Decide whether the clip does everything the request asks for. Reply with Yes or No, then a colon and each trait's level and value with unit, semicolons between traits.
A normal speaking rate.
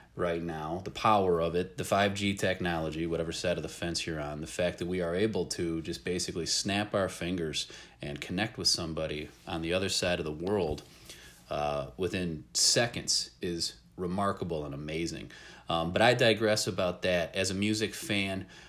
Yes: average, 180 wpm